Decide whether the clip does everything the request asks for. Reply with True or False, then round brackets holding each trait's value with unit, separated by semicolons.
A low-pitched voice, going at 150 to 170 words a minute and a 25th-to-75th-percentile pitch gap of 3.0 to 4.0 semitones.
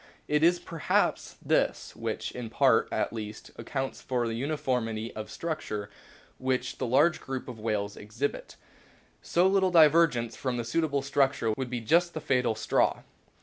False (130 Hz; 160 wpm; 5.1 semitones)